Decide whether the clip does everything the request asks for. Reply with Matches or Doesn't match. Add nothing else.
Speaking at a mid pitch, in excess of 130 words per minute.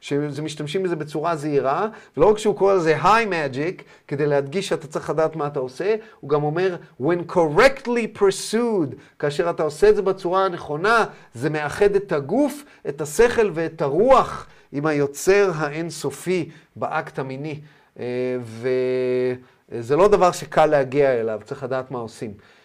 Matches